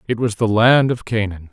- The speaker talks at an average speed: No, fast, 235 wpm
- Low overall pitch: Yes, low, 110 Hz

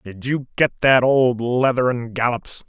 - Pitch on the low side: Yes, low, 125 Hz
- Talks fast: No, average, 180 wpm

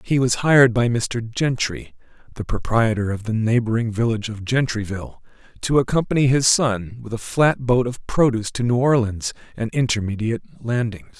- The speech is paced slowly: No, average, 160 wpm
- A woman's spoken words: No, male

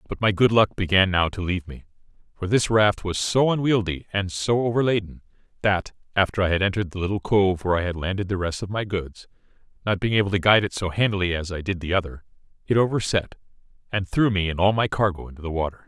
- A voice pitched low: Yes, very low, 95 Hz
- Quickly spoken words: Yes, fast, 225 wpm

